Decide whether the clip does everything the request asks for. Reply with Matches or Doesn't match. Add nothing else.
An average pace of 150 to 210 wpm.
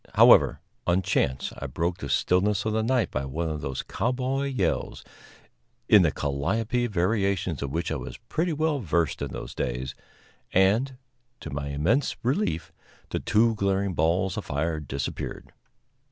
Matches